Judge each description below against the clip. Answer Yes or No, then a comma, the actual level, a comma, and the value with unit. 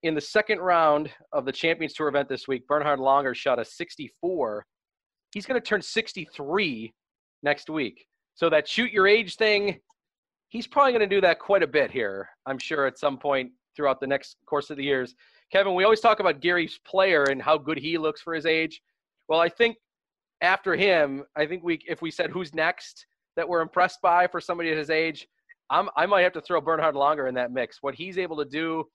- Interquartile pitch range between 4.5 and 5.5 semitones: Yes, average, 4.8 semitones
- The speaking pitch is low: No, medium, 160 Hz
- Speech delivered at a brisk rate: Yes, fast, 215 wpm